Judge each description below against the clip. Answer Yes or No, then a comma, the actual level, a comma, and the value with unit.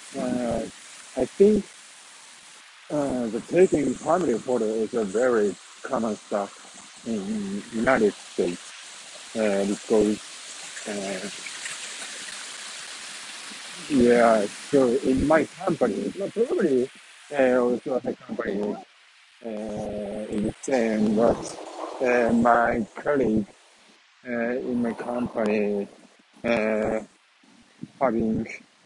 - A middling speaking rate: No, slow, 85 wpm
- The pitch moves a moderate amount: Yes, average, 3.5 semitones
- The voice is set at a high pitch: No, low, 120 Hz